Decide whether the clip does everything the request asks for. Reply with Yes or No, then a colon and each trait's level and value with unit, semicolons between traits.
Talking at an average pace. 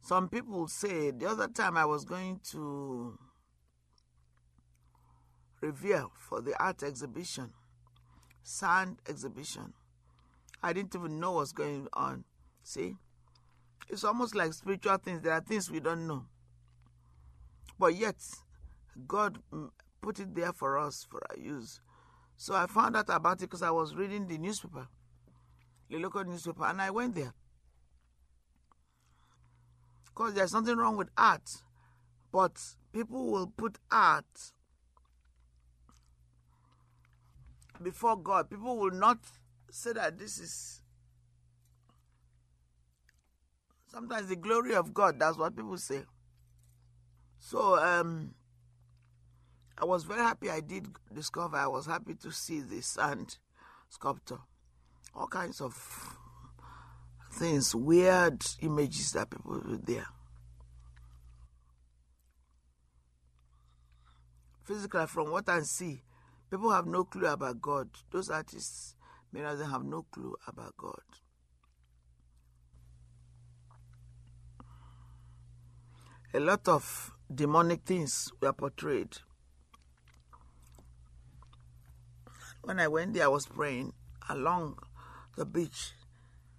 No: slow, 110 wpm